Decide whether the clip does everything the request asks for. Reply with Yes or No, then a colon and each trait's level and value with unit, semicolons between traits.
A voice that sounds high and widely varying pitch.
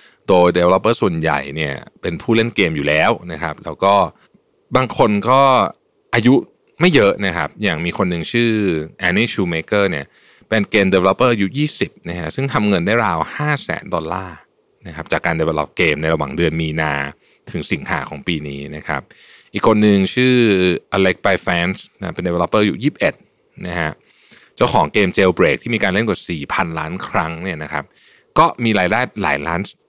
No: very low, 95 Hz; wide, 6.1 semitones